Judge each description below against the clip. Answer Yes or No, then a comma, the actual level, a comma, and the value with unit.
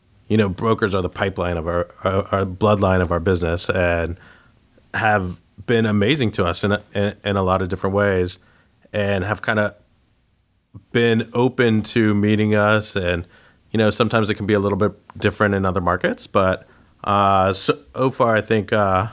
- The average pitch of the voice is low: Yes, low, 100 Hz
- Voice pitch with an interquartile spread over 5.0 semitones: No, narrow, 2.4 semitones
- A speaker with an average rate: Yes, average, 175 wpm